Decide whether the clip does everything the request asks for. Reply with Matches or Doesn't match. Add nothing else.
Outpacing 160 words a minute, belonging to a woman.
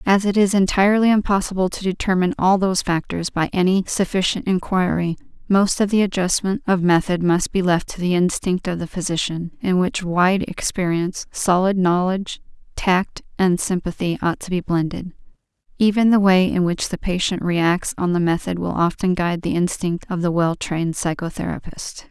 Matches